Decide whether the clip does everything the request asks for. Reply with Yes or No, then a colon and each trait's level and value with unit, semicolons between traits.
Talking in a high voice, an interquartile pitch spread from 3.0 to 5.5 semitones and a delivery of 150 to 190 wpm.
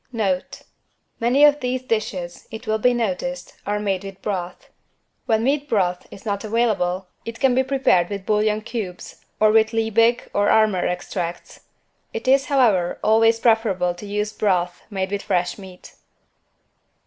Yes: high, 215 Hz; average, 3.5 semitones; average, 155 wpm